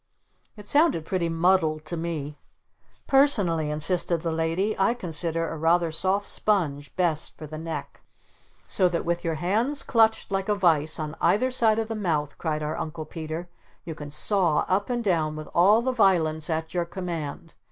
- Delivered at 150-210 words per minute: Yes, average, 175 wpm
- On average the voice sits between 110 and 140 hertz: No, medium, 170 Hz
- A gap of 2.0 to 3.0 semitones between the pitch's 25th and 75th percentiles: No, average, 3.8 semitones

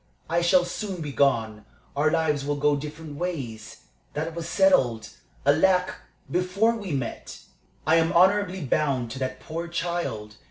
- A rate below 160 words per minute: Yes, average, 150 wpm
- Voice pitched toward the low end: No, medium, 155 Hz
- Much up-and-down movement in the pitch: No, average, 4.6 semitones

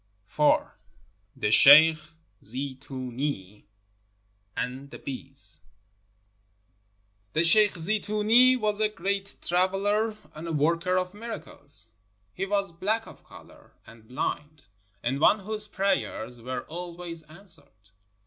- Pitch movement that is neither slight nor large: No, wide, 6.8 semitones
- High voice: No, medium, 165 Hz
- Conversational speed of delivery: No, slow, 110 wpm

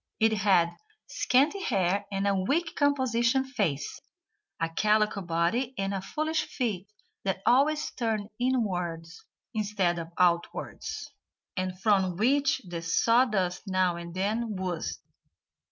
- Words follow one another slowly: Yes, slow, 120 wpm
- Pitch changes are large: Yes, wide, 5.7 semitones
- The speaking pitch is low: No, high, 200 Hz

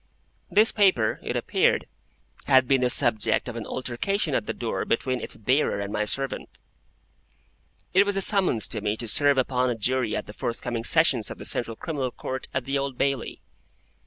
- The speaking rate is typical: Yes, average, 190 wpm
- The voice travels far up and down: No, average, 3.3 semitones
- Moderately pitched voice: No, low, 130 Hz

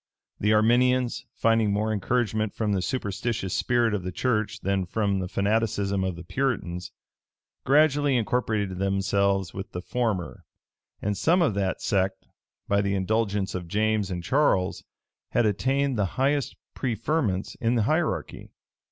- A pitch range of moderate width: Yes, average, 3.9 semitones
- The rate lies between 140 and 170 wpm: Yes, average, 145 wpm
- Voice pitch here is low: Yes, low, 105 Hz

